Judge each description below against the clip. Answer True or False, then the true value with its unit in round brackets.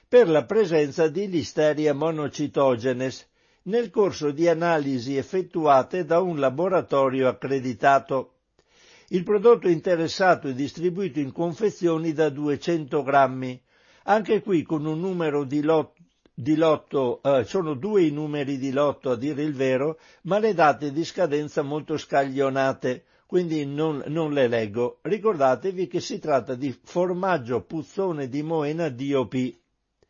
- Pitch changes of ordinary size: True (4.2 semitones)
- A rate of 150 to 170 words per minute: False (135 wpm)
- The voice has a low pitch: False (155 Hz)